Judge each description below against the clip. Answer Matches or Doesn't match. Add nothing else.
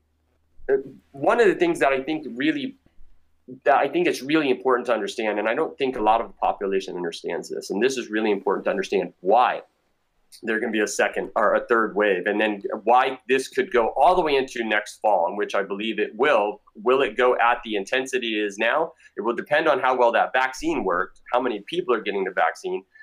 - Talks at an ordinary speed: Doesn't match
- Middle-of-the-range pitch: Doesn't match